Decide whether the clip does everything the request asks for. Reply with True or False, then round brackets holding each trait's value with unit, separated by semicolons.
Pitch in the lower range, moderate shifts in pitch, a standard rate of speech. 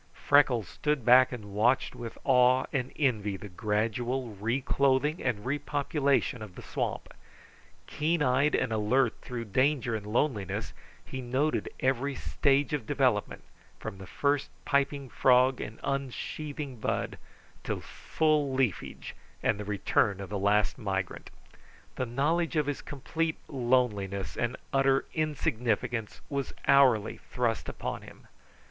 False (130 Hz; 4.4 semitones; 130 wpm)